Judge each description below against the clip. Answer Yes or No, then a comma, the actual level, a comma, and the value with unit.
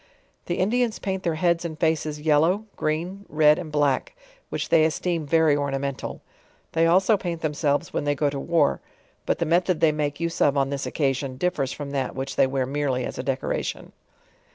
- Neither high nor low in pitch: Yes, medium, 155 Hz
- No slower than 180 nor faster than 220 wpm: Yes, average, 195 wpm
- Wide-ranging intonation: No, average, 3.3 semitones